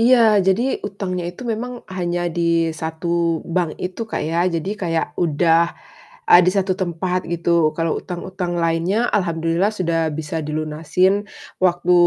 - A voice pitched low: No, medium, 175 Hz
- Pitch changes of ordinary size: No, narrow, 2.2 semitones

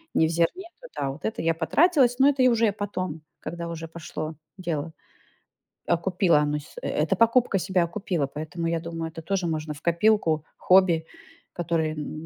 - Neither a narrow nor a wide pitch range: Yes, average, 3.7 semitones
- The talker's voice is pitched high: No, medium, 170 Hz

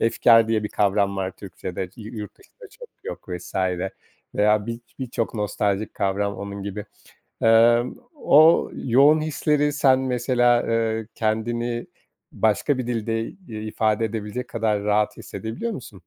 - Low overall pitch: Yes, low, 115 Hz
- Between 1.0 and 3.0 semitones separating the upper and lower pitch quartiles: Yes, average, 2.7 semitones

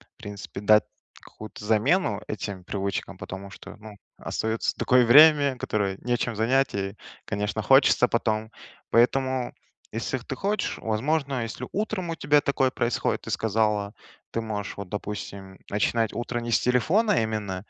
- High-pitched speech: No, low, 110 Hz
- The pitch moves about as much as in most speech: Yes, average, 4.1 semitones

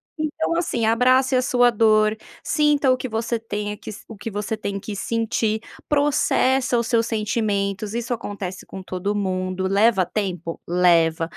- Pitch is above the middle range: Yes, high, 220 Hz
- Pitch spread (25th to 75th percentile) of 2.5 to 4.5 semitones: Yes, average, 3.6 semitones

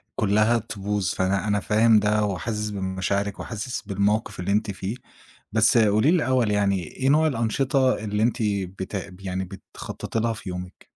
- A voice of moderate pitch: No, low, 105 Hz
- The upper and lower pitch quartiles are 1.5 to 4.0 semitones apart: Yes, narrow, 2.5 semitones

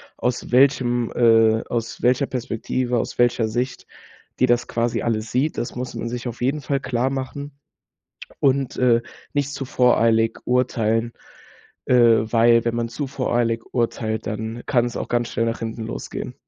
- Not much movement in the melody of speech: Yes, narrow, 1.8 semitones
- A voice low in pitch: Yes, low, 120 Hz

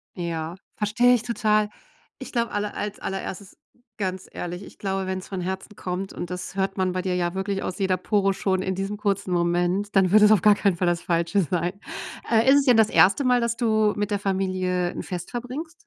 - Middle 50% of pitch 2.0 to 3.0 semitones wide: Yes, narrow, 2.6 semitones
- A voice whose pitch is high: Yes, high, 195 Hz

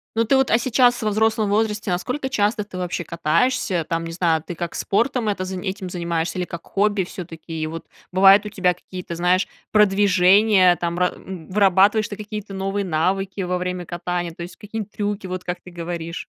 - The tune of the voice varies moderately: Yes, average, 3.1 semitones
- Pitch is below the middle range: No, medium, 185 Hz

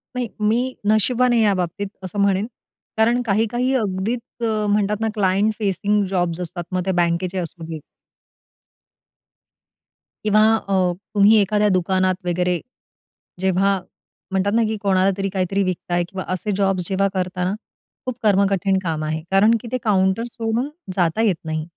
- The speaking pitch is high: Yes, high, 195 Hz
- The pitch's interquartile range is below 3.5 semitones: Yes, average, 2.8 semitones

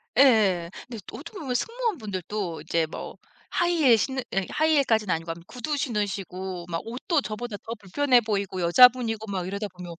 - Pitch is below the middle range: No, high, 220 Hz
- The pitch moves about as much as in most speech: No, wide, 5.8 semitones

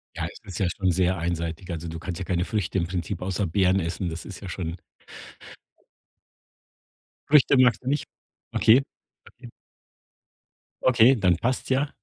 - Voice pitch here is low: Yes, very low, 95 Hz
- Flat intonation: No, average, 4.9 semitones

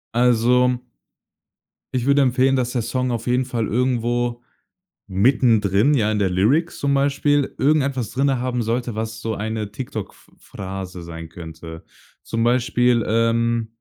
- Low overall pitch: Yes, low, 120 Hz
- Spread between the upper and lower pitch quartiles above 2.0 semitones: Yes, average, 2.9 semitones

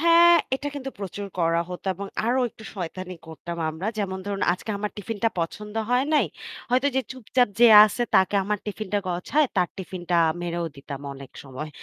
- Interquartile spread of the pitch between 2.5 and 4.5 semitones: No, average, 5.1 semitones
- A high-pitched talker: Yes, high, 200 Hz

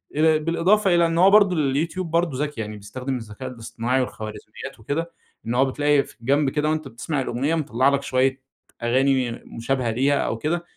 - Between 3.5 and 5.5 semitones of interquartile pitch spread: Yes, average, 4.1 semitones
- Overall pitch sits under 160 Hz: Yes, low, 135 Hz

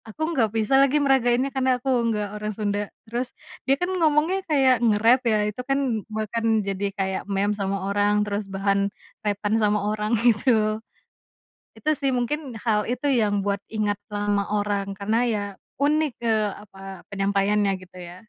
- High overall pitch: Yes, high, 215 Hz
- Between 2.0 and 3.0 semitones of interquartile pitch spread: No, average, 3.7 semitones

